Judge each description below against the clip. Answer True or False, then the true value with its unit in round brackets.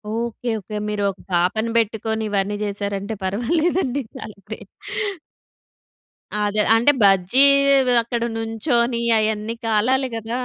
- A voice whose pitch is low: False (220 Hz)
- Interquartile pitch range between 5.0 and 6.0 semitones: False (2.5 semitones)